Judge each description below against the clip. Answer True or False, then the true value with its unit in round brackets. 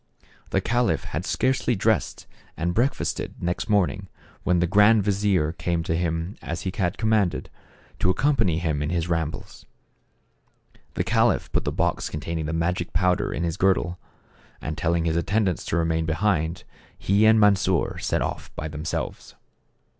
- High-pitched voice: False (90 Hz)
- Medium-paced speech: True (160 wpm)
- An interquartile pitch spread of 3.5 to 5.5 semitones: True (3.8 semitones)